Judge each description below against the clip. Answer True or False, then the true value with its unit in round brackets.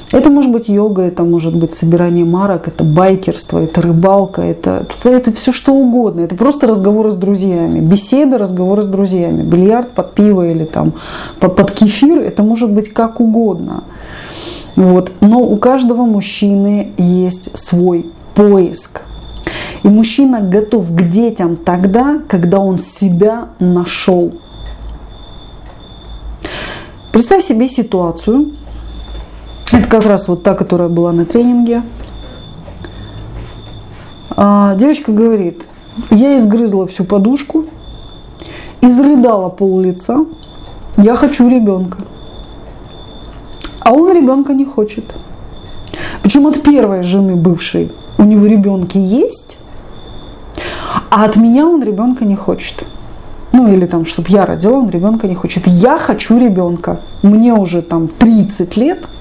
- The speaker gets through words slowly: False (125 wpm)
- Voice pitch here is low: False (200 Hz)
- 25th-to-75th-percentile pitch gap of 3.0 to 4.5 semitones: False (5.2 semitones)